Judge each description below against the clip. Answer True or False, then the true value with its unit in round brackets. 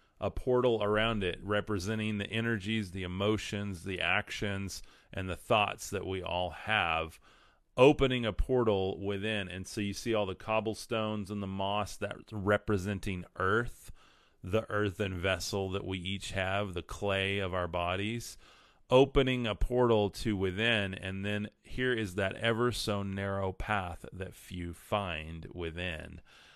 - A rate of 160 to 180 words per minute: False (145 wpm)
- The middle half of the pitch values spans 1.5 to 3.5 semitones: True (2.4 semitones)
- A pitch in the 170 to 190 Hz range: False (100 Hz)